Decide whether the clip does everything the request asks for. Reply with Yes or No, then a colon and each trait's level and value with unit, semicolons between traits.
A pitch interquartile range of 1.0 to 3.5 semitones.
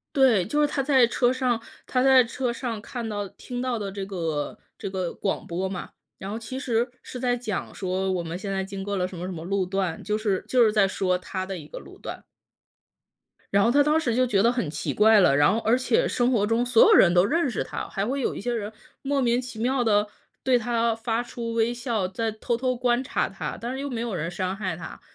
No: average, 4.2 semitones